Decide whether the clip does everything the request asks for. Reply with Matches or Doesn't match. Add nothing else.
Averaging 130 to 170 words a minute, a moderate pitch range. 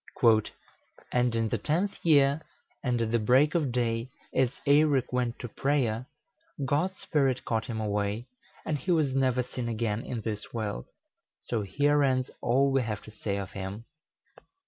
Matches